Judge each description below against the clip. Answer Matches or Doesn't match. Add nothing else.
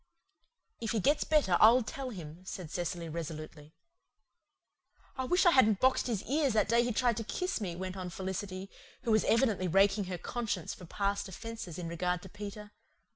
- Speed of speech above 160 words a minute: Matches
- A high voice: Matches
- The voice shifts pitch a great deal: Doesn't match